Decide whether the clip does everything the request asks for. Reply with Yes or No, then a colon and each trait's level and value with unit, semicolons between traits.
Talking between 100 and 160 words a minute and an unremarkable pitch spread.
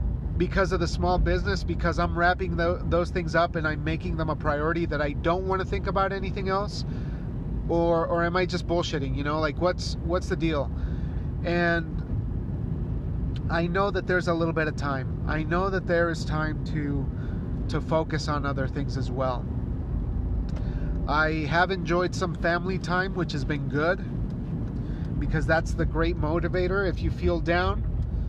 No: average, 175 wpm; average, 3.7 semitones